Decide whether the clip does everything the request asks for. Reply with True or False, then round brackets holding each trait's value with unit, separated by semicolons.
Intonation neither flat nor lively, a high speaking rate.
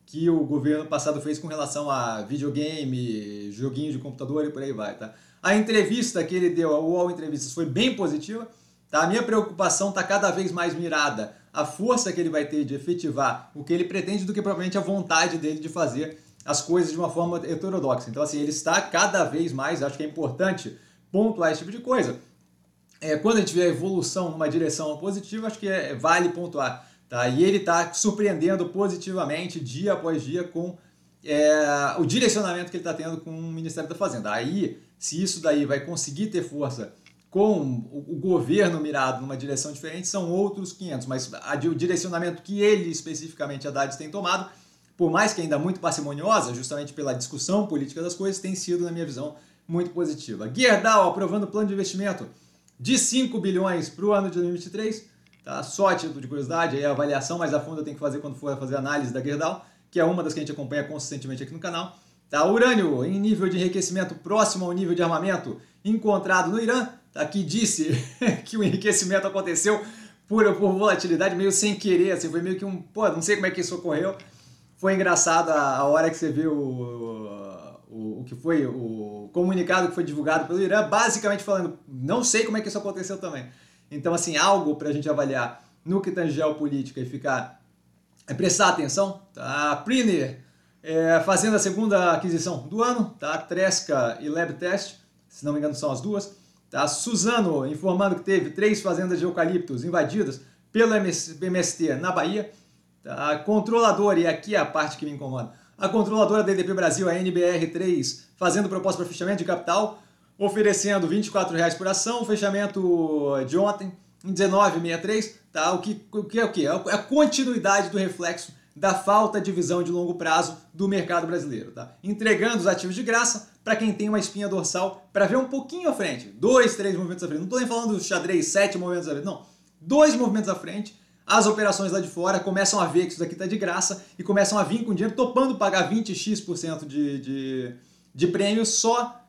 True (4.9 semitones; 195 wpm)